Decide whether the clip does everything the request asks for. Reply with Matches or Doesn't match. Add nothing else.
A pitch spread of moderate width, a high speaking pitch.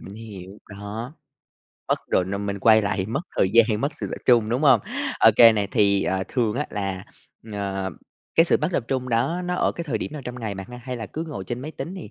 Doesn't match